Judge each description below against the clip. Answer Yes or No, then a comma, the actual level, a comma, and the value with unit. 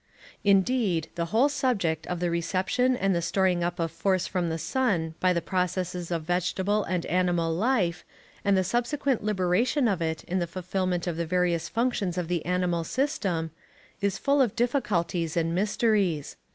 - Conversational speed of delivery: Yes, average, 170 wpm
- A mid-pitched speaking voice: Yes, medium, 180 Hz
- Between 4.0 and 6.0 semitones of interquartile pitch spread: No, average, 3.6 semitones